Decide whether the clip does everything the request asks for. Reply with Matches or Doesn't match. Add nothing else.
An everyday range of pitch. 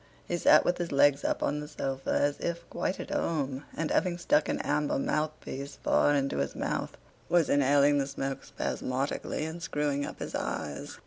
Doesn't match